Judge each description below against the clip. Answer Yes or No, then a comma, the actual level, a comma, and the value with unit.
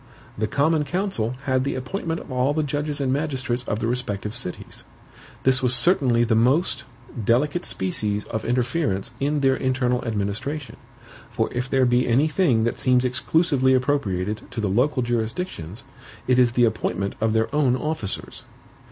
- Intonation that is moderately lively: Yes, average, 4.0 semitones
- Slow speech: No, average, 160 wpm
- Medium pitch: No, low, 125 Hz